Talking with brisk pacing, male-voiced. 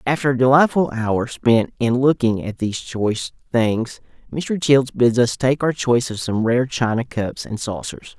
No: average, 185 wpm; male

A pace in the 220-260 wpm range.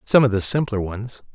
Yes: fast, 225 wpm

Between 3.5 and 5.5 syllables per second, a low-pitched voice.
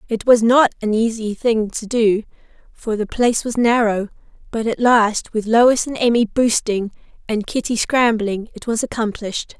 No: 4.7 syllables/s; high, 225 Hz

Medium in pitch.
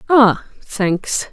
No: high, 220 Hz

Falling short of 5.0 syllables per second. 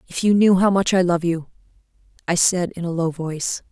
No: 5.5 syllables/s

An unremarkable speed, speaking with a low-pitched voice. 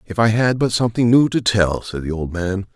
No: fast, 260 wpm; low, 105 Hz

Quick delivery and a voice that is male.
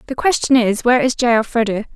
No: fast, 215 wpm; female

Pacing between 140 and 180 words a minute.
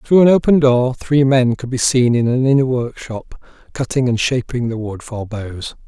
No: fast, 205 wpm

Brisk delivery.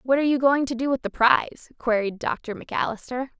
Yes: fast, 210 wpm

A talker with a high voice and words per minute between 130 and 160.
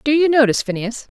No: very high, 260 Hz; average, 200 wpm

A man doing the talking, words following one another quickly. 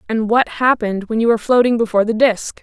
No: female; fast, 230 wpm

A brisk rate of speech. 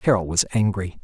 No: average, 175 wpm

